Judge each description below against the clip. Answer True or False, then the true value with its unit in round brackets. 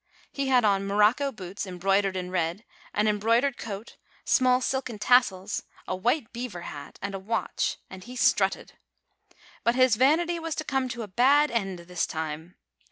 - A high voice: True (215 Hz)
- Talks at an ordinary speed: True (170 wpm)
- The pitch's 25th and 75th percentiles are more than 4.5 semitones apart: True (5.1 semitones)